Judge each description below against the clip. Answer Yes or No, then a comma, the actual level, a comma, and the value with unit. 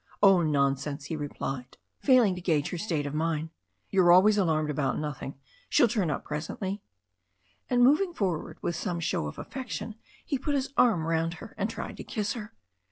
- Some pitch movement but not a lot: No, wide, 5.9 semitones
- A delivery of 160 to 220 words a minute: Yes, average, 180 wpm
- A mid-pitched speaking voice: Yes, medium, 170 Hz